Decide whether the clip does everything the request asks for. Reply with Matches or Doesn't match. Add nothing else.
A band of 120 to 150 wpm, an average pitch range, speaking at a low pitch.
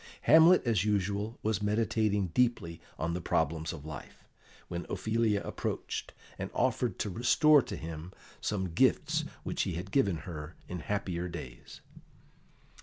Matches